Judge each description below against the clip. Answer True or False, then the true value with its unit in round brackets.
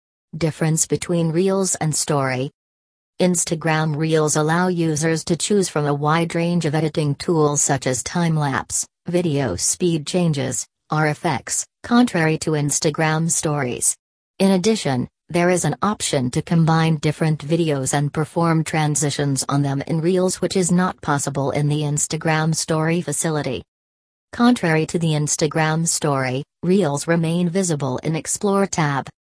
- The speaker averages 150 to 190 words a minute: False (135 wpm)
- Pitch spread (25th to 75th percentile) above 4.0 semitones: False (2.9 semitones)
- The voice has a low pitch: False (155 Hz)